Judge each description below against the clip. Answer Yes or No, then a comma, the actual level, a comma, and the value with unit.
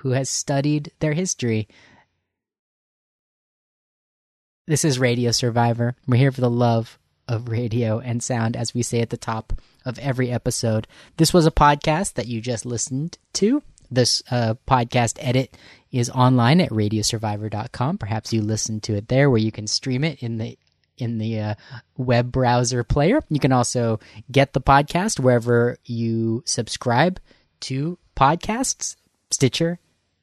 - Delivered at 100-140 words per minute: No, average, 150 wpm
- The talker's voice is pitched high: No, low, 120 Hz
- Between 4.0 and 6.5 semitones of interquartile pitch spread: No, average, 3.3 semitones